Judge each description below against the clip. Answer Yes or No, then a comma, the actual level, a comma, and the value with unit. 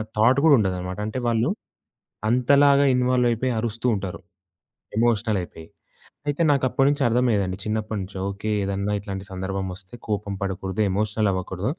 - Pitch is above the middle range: No, low, 105 Hz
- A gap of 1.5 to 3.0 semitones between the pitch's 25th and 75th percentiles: No, average, 4.2 semitones